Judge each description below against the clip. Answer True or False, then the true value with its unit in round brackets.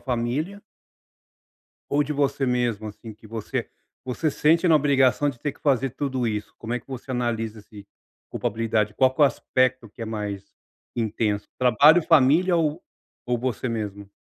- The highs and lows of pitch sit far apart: False (4.2 semitones)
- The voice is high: False (125 Hz)